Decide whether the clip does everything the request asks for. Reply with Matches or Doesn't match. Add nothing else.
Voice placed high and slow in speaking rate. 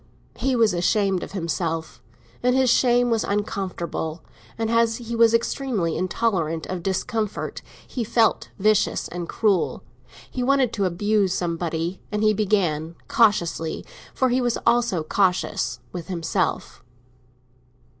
Matches